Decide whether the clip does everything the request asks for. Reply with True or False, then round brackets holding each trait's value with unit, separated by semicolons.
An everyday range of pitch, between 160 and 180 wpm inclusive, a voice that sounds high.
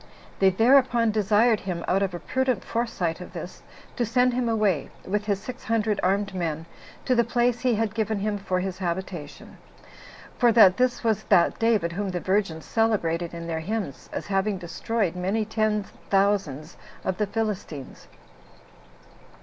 True (3.8 semitones; 165 wpm; 200 Hz)